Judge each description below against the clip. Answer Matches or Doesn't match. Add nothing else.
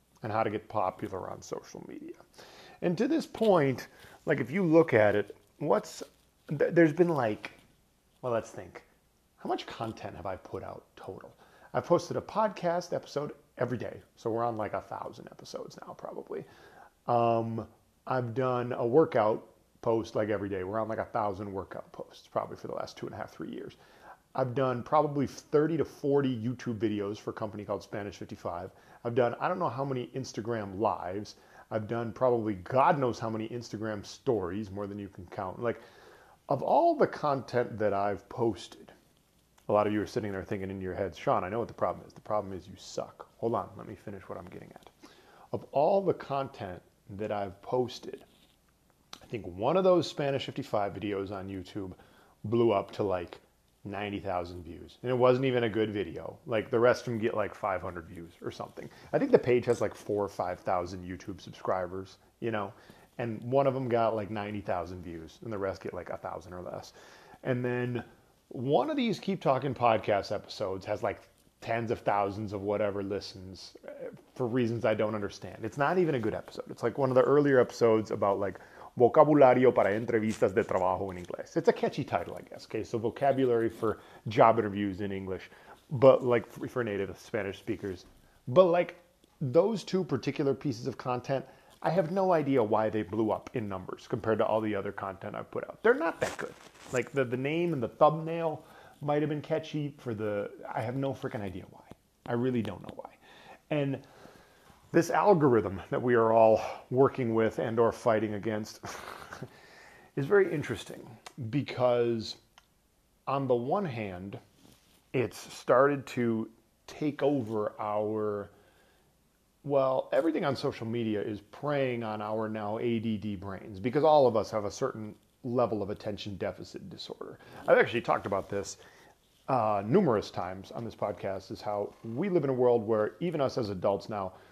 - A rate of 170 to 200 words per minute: Matches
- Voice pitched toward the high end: Doesn't match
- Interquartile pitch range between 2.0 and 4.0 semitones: Doesn't match